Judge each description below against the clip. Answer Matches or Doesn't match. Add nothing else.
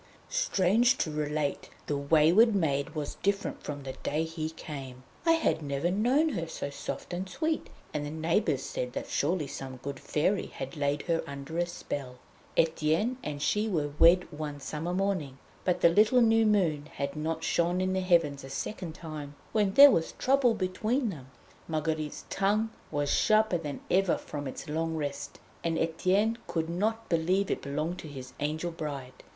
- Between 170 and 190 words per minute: Matches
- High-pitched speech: Doesn't match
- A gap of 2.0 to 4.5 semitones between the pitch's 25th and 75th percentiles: Doesn't match